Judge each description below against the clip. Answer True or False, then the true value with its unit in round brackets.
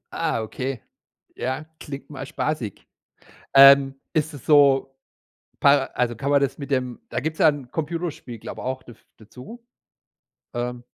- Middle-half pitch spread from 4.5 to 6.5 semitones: False (2.9 semitones)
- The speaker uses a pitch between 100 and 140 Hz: True (135 Hz)